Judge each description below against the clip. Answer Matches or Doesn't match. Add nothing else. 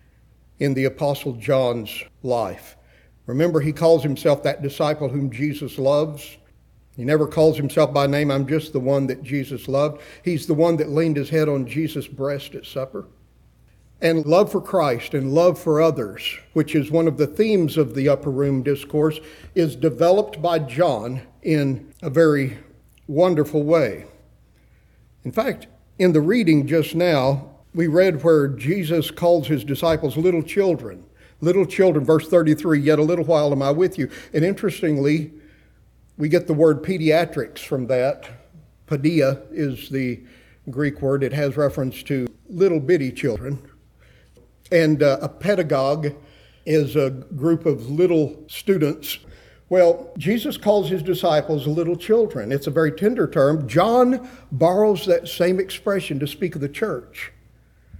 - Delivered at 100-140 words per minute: Doesn't match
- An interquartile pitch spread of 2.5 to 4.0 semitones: Matches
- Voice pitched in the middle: Matches